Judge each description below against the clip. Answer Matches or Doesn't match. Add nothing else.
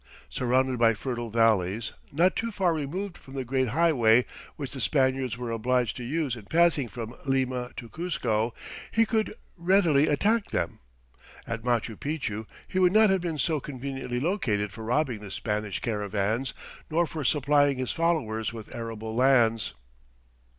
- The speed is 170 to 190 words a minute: Doesn't match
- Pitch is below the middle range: Matches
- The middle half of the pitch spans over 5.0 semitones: Matches